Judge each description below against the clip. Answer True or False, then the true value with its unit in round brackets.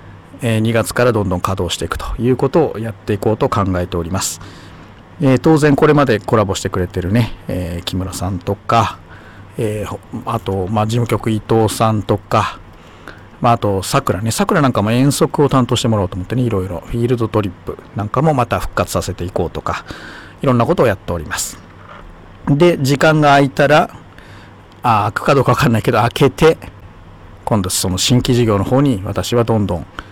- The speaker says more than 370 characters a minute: True (380 characters per minute)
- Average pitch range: True (4.9 semitones)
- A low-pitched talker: True (110 Hz)